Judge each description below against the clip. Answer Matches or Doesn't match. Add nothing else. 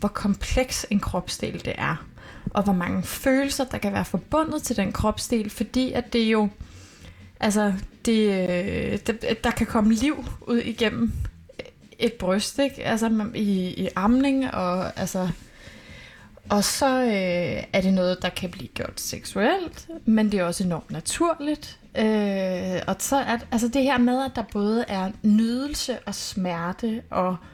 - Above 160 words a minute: Doesn't match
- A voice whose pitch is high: Matches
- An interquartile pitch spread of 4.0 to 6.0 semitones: Matches